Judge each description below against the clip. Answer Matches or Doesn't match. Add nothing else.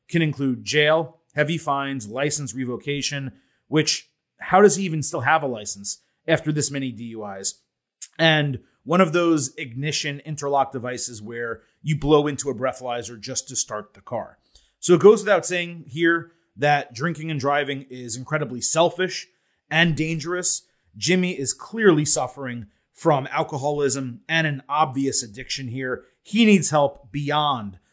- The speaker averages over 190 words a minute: Doesn't match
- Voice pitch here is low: Doesn't match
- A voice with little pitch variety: Doesn't match